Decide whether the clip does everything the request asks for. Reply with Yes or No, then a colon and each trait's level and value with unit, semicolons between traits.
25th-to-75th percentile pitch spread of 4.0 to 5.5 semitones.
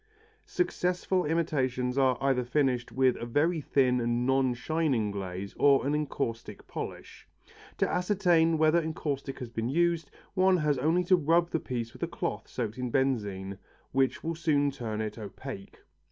Yes: average, 5.0 semitones